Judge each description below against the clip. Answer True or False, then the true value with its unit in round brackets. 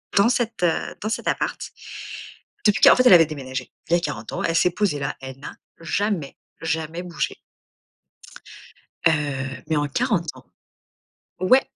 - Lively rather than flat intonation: True (5.7 semitones)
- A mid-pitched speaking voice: True (165 Hz)